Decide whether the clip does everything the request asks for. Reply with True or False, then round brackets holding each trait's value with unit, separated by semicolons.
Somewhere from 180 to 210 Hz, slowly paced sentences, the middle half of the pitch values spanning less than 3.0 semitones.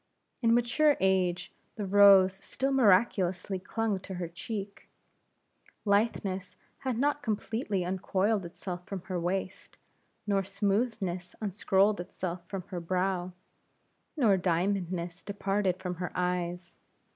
True (190 Hz; 120 wpm; 2.4 semitones)